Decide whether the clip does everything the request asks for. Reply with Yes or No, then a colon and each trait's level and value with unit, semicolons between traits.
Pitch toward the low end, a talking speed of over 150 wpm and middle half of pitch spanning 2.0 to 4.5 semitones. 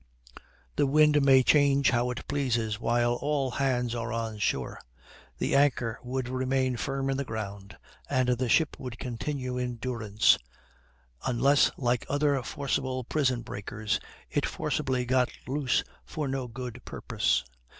No: low, 125 Hz; average, 140 wpm; narrow, 2.4 semitones